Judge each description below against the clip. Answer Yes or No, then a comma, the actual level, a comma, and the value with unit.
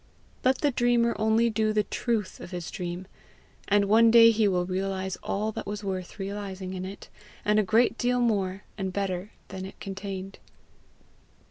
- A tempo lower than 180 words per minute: Yes, average, 170 wpm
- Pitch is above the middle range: Yes, high, 200 Hz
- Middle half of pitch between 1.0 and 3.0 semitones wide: Yes, average, 2.7 semitones